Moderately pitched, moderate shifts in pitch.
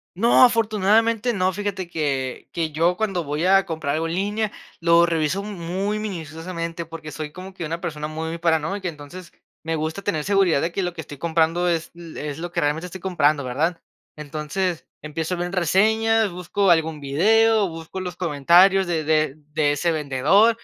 Yes: medium, 170 Hz; average, 3.6 semitones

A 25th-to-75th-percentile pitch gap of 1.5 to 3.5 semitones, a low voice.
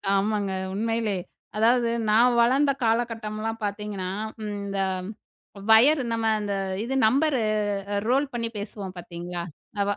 No: average, 3.0 semitones; high, 220 Hz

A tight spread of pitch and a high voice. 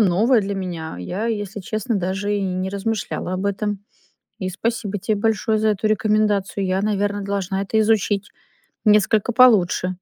Yes: narrow, 2.1 semitones; high, 205 Hz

